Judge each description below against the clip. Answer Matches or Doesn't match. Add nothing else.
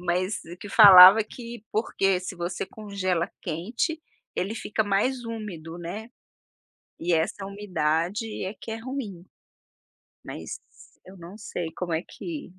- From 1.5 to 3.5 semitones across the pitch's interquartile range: Doesn't match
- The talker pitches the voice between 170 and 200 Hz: Matches